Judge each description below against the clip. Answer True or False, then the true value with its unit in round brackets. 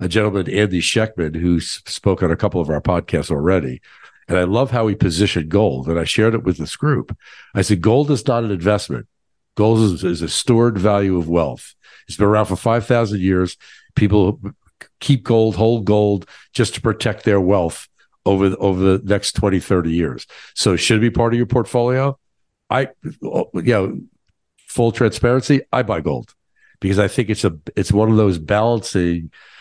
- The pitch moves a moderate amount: True (3.9 semitones)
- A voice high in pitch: False (105 Hz)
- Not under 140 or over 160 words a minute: False (185 wpm)